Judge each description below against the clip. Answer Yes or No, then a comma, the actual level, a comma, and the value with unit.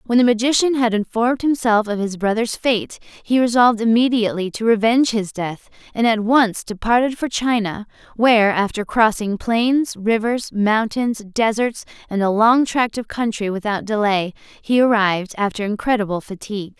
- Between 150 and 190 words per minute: Yes, average, 155 wpm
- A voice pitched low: No, high, 220 Hz